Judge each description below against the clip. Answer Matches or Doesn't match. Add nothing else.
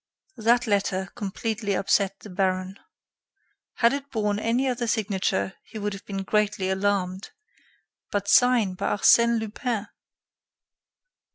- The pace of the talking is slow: Matches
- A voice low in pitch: Doesn't match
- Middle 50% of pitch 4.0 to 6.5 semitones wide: Doesn't match